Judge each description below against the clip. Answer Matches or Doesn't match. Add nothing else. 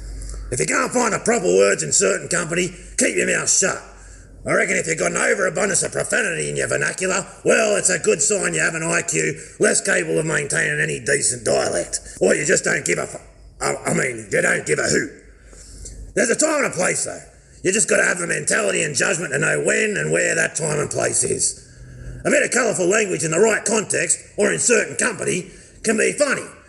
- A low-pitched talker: Doesn't match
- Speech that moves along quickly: Matches